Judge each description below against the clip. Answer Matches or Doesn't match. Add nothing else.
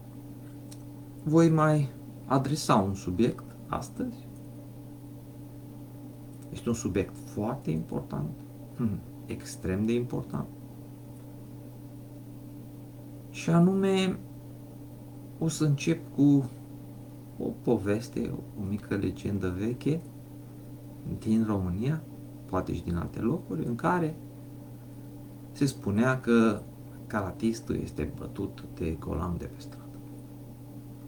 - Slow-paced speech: Matches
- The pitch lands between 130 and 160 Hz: Doesn't match